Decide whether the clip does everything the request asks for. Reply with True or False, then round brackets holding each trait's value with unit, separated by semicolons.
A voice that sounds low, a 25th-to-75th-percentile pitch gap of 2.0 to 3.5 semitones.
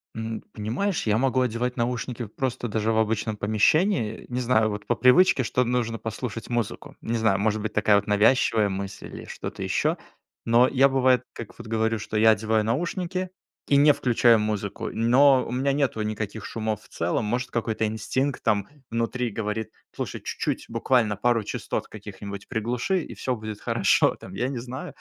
True (115 Hz; 2.8 semitones)